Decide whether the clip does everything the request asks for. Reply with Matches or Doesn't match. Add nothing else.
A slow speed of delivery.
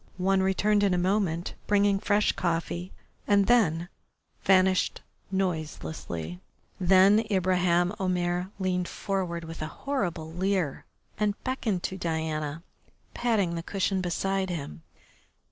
Matches